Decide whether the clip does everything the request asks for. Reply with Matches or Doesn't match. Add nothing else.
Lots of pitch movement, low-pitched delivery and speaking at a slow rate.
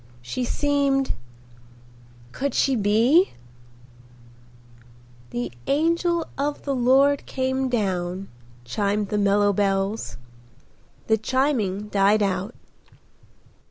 Doesn't match